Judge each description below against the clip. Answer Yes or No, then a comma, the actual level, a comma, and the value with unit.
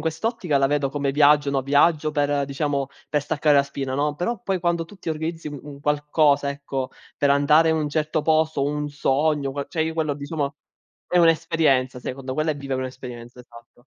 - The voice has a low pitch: No, medium, 145 Hz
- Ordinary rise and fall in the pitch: No, narrow, 2.3 semitones